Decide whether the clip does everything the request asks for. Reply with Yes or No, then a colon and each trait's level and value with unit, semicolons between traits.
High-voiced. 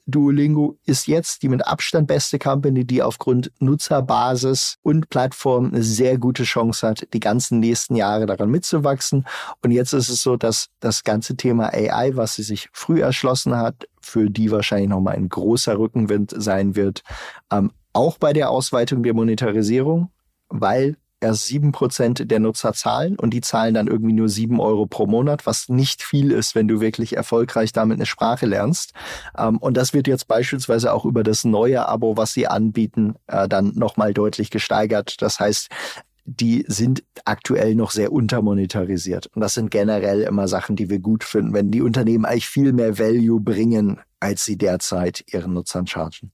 No: low, 115 Hz